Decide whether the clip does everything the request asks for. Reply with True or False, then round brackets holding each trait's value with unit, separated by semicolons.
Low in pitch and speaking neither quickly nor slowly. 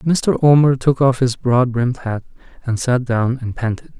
True (125 Hz; 195 wpm)